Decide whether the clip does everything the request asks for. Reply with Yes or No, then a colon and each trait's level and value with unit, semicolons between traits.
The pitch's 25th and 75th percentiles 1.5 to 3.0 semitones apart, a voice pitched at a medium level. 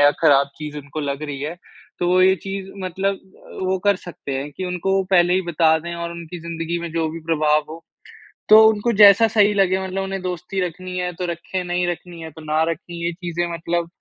Yes: average, 2.7 semitones; medium, 175 Hz